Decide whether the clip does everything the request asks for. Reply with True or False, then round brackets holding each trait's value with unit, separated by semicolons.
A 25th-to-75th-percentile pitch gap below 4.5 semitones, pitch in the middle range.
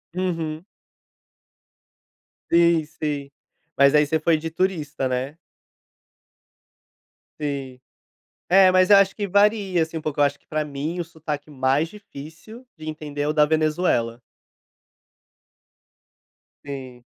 True (3.2 semitones; 155 Hz)